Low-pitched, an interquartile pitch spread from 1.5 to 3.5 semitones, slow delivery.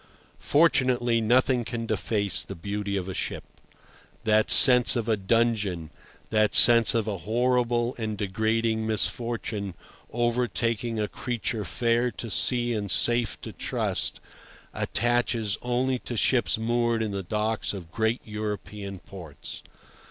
Yes: low, 115 Hz; narrow, 2.5 semitones; slow, 130 wpm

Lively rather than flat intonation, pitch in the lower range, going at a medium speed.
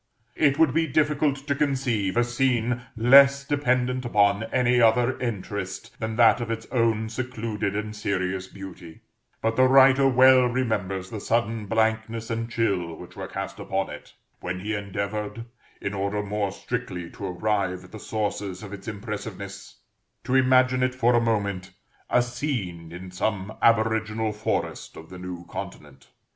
No: average, 4.0 semitones; low, 110 Hz; average, 155 wpm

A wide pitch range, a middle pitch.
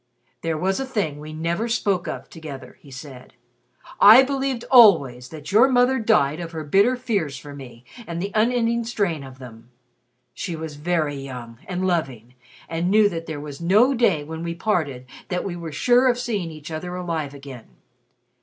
Yes: wide, 6.7 semitones; medium, 170 Hz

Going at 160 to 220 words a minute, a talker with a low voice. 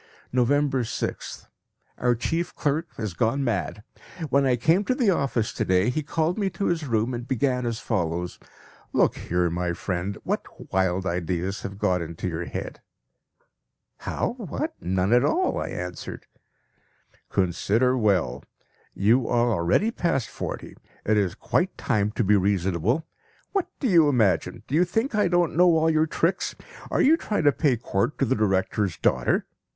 Yes: average, 165 wpm; low, 120 Hz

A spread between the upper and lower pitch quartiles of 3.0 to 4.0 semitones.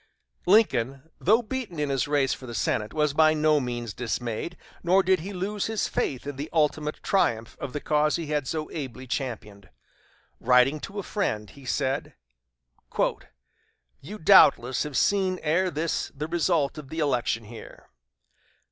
No: average, 5.0 semitones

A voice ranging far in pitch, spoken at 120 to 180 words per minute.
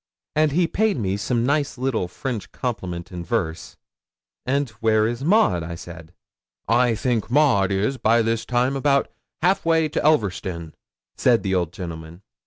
Yes: wide, 6.8 semitones; average, 155 wpm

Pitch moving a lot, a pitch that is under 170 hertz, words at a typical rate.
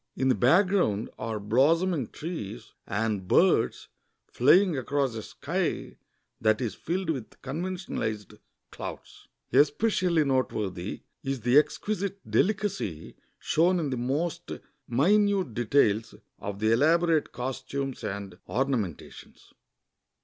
No: wide, 7.6 semitones; low, 135 Hz; slow, 105 wpm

